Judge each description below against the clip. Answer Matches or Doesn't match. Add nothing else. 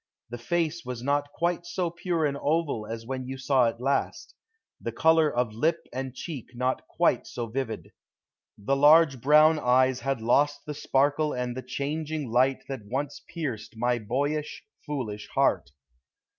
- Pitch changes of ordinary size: Matches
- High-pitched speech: Doesn't match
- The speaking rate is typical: Matches